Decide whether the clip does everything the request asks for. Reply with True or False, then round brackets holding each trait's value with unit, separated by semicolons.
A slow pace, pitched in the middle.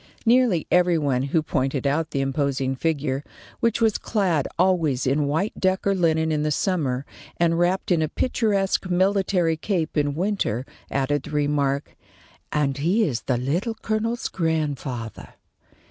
False (150 wpm; 160 Hz)